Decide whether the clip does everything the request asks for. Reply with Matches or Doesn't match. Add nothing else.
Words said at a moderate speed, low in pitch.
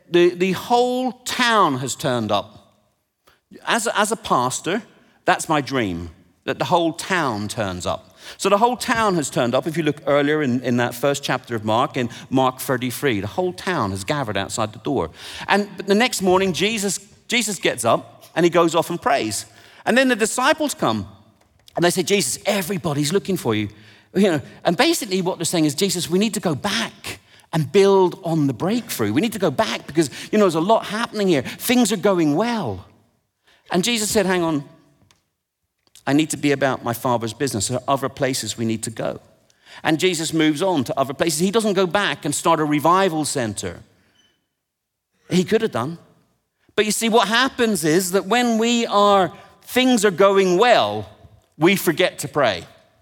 Doesn't match